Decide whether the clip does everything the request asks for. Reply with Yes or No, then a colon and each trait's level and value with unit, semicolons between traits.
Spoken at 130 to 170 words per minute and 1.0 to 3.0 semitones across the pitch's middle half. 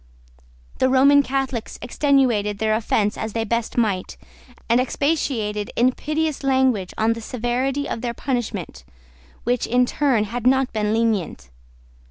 No: average, 140 wpm; average, 3.5 semitones